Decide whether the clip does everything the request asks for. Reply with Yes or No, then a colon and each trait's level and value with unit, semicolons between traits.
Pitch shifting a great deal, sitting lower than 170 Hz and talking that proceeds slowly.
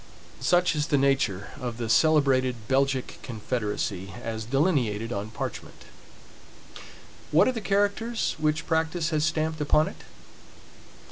Yes: wide, 5.8 semitones; medium, 140 Hz; slow, 125 wpm